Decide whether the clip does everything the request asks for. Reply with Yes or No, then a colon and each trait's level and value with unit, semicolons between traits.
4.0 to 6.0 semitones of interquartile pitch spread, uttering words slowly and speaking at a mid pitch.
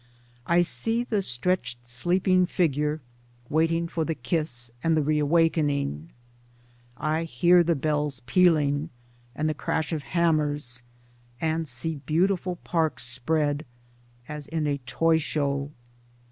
No: average, 3.0 semitones; slow, 130 wpm; medium, 155 Hz